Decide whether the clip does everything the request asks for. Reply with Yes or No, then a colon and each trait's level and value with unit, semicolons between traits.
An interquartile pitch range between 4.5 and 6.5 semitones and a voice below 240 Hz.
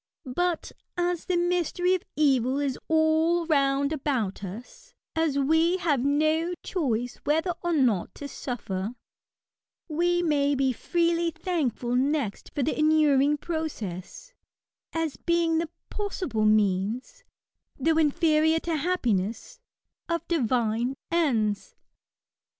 No: average, 5.1 semitones; very high, 305 Hz